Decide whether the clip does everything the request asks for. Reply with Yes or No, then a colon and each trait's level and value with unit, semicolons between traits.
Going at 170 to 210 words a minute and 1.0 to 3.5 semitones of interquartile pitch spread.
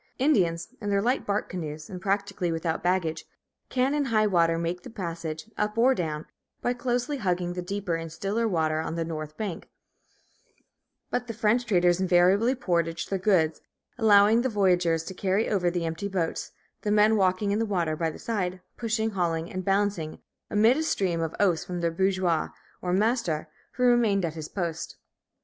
No: average, 180 wpm; average, 4.2 semitones